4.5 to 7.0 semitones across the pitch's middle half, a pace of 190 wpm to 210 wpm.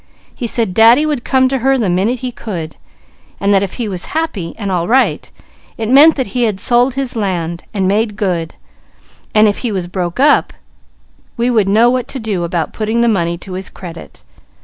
Yes: average, 4.9 semitones; fast, 205 wpm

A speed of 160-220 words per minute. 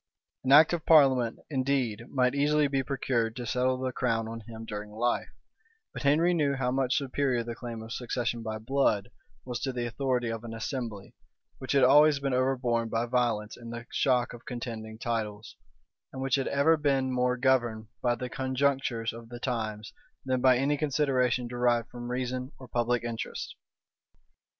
Yes: average, 175 wpm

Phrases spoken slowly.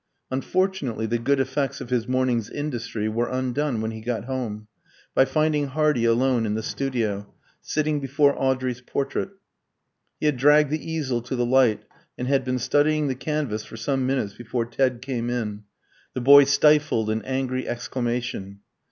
No: average, 165 wpm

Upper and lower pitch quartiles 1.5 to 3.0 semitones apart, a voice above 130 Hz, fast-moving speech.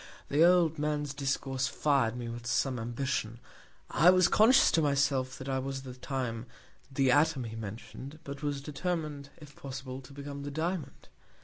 No: narrow, 2.6 semitones; medium, 140 Hz; average, 175 wpm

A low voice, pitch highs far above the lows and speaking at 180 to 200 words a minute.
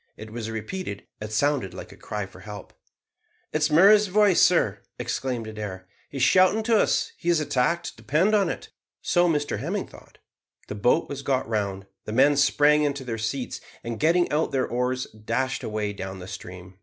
Yes: low, 130 Hz; wide, 6.3 semitones; average, 190 wpm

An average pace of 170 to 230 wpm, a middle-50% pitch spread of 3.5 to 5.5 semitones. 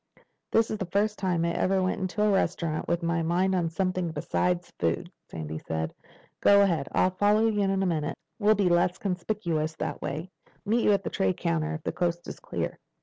No: fast, 205 wpm; average, 3.1 semitones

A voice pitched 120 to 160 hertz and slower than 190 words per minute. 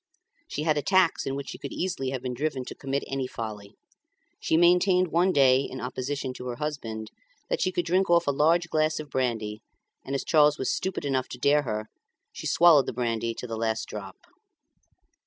No: medium, 140 Hz; fast, 205 wpm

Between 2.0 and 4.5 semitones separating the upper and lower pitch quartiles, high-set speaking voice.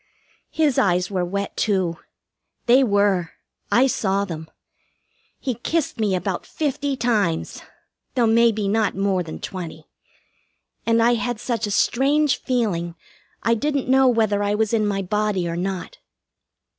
Yes: average, 4.2 semitones; high, 210 Hz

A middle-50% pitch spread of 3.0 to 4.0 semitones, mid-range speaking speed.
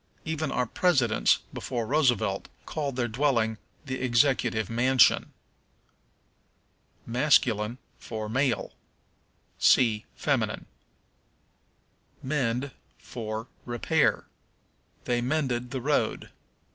No: average, 3.3 semitones; slow, 80 wpm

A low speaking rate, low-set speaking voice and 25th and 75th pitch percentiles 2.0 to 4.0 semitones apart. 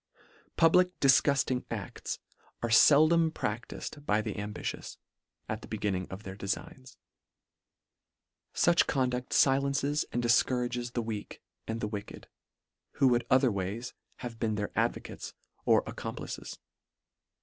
No: slow, 125 wpm; low, 120 Hz; average, 4.4 semitones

